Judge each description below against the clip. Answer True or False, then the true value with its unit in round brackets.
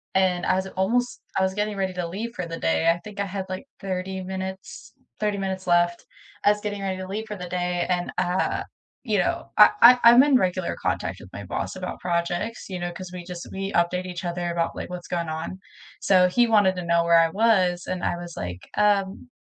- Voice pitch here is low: False (185 Hz)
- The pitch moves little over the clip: True (2.3 semitones)